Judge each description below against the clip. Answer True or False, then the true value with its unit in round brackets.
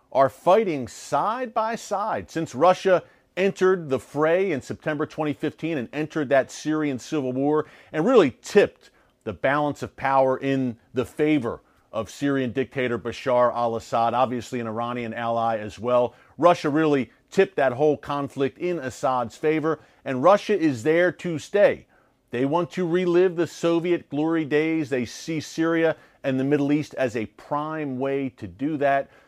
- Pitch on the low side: False (145 Hz)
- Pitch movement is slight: False (4.1 semitones)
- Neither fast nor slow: True (160 wpm)